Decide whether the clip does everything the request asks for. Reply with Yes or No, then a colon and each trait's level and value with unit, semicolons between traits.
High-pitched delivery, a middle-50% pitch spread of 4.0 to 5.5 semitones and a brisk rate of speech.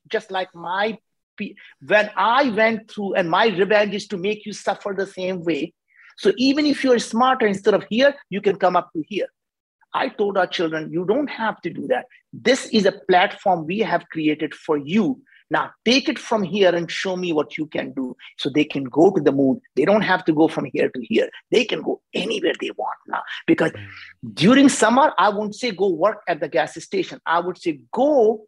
Yes: high, 205 Hz; average, 4.7 semitones; fast, 215 wpm